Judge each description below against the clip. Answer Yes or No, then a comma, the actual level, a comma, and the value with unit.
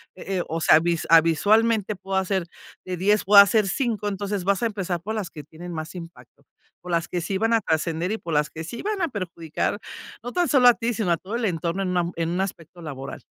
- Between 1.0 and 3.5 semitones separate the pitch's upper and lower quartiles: No, average, 4.2 semitones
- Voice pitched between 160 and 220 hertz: Yes, medium, 185 Hz